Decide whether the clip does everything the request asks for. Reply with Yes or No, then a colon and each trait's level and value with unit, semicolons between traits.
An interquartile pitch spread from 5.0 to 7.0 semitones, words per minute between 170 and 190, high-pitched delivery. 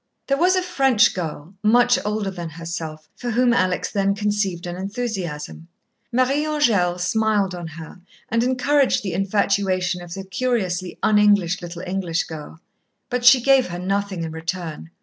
No: average, 5.3 semitones; average, 160 wpm; high, 195 Hz